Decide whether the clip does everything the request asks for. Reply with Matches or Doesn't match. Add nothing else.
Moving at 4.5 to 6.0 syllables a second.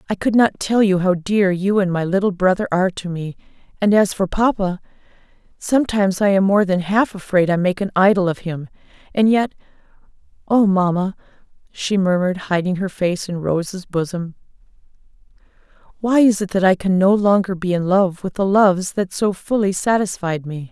Matches